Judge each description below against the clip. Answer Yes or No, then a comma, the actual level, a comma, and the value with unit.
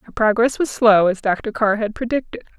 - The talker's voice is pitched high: Yes, high, 230 Hz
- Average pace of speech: No, fast, 210 wpm